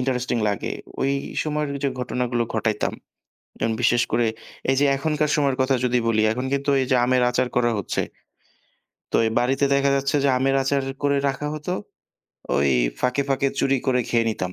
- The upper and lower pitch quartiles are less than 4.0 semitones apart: Yes, narrow, 2.4 semitones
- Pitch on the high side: No, low, 130 Hz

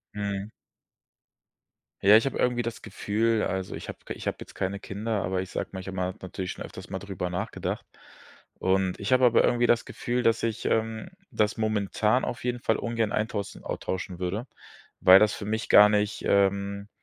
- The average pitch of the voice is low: Yes, low, 105 Hz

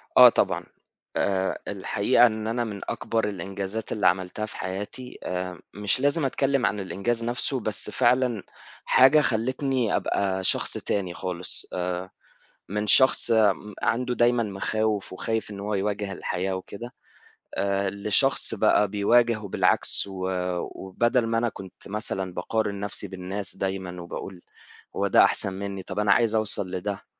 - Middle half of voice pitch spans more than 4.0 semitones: No, average, 3.3 semitones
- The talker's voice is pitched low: Yes, low, 105 Hz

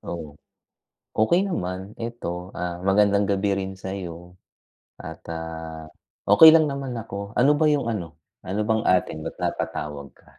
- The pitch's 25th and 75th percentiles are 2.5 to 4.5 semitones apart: No, average, 5.1 semitones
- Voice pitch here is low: Yes, low, 100 Hz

